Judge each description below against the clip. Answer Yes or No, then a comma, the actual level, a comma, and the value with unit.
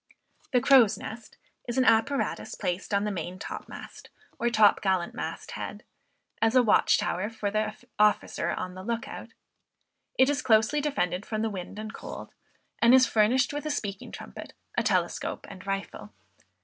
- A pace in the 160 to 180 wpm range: Yes, average, 170 wpm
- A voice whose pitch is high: Yes, high, 215 Hz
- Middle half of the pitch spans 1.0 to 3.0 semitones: No, average, 3.9 semitones